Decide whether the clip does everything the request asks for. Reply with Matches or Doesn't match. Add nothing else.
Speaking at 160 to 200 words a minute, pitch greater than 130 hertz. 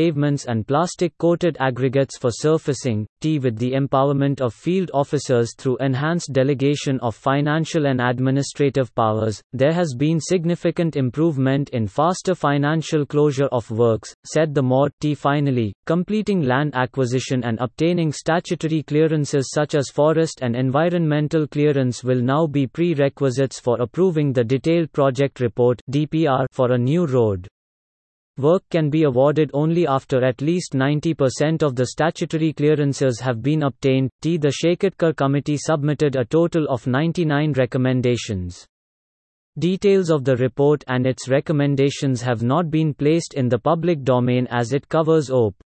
Doesn't match